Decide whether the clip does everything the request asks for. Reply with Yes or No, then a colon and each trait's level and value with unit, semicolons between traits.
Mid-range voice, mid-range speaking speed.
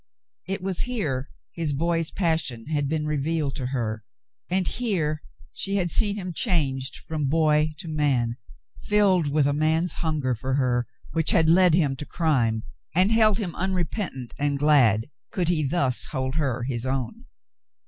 Yes: medium, 155 Hz; average, 160 wpm